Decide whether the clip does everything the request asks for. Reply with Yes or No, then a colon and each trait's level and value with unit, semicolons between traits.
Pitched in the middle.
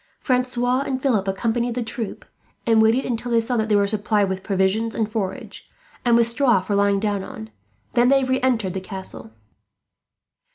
No: high, 225 Hz